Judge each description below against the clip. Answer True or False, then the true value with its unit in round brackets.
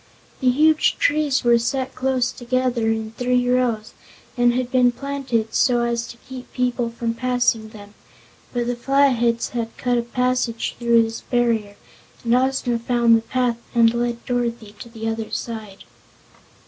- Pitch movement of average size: False (1.5 semitones)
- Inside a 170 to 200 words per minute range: False (160 wpm)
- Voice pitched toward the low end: False (240 Hz)